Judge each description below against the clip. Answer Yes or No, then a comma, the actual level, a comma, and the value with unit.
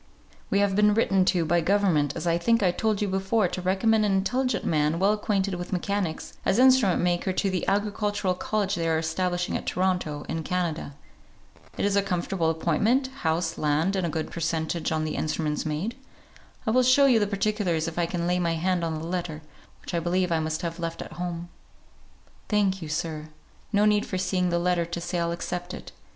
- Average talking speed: No, fast, 210 wpm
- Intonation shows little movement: No, average, 3.3 semitones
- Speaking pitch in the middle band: Yes, medium, 180 Hz